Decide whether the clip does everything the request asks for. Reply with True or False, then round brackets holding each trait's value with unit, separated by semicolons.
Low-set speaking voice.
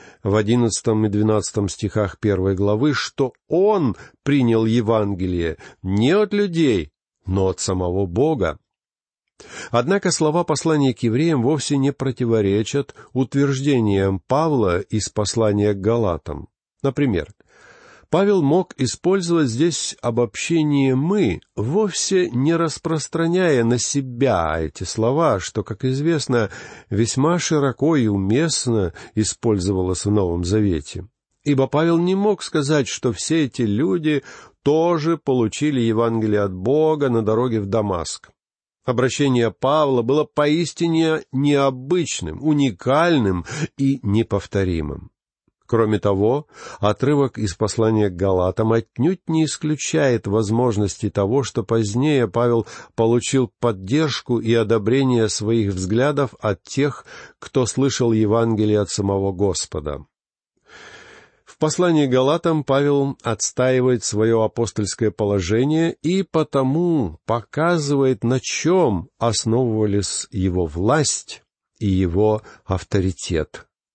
True (120 Hz)